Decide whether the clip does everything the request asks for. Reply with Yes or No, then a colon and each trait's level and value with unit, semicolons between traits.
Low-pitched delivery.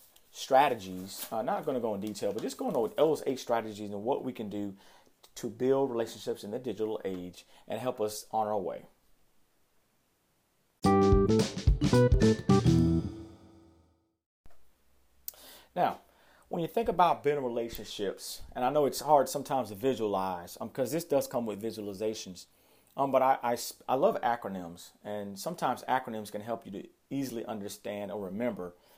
Yes: low, 110 Hz